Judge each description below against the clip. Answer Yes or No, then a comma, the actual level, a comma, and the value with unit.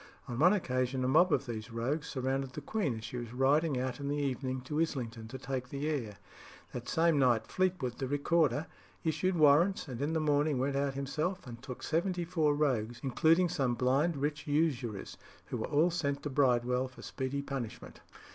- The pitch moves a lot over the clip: No, average, 3.6 semitones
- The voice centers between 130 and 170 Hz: Yes, medium, 140 Hz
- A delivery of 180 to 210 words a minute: Yes, average, 195 wpm